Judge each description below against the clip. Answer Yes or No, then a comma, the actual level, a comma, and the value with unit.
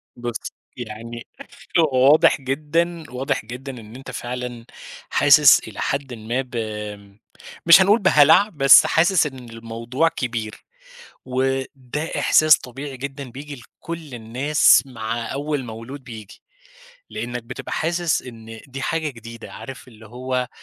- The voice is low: Yes, low, 130 Hz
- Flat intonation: No, average, 3.8 semitones